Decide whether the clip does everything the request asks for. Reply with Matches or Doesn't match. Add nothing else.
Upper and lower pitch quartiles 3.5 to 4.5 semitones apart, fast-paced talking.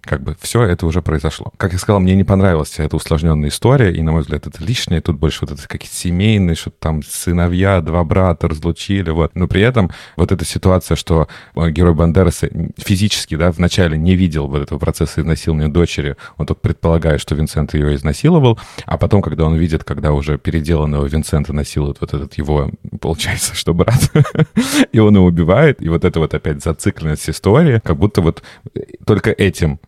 Matches